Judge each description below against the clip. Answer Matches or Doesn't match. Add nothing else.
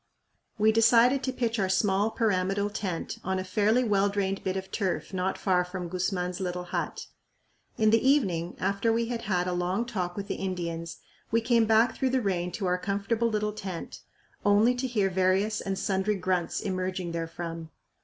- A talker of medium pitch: Doesn't match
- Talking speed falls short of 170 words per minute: Doesn't match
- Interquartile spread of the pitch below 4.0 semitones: Matches